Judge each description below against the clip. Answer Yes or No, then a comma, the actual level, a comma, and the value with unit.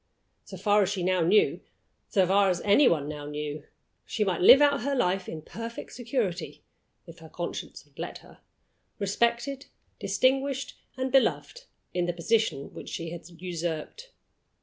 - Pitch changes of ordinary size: No, wide, 6.3 semitones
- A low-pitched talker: No, high, 200 Hz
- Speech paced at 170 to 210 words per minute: No, average, 160 wpm